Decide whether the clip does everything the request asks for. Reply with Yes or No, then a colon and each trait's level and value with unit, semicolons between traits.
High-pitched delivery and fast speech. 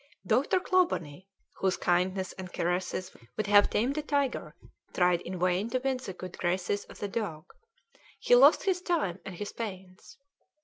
No: high, 195 Hz; average, 165 wpm